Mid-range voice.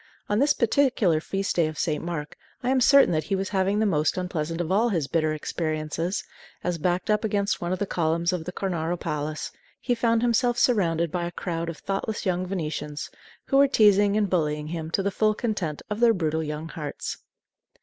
Yes: medium, 180 Hz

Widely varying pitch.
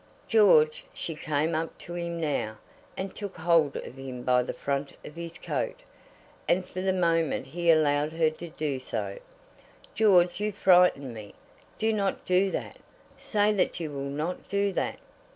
No: average, 4.3 semitones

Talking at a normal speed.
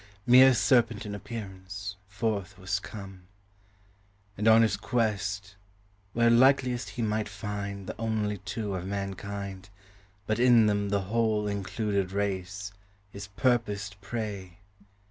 No: slow, 125 wpm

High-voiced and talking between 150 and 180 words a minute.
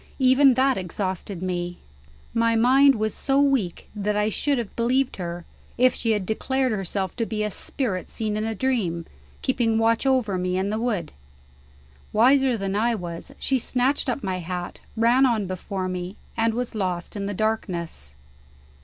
Yes: high, 220 Hz; average, 170 wpm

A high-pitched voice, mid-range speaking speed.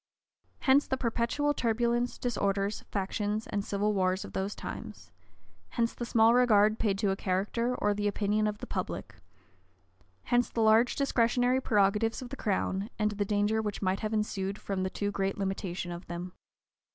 Yes: high, 210 Hz; average, 170 wpm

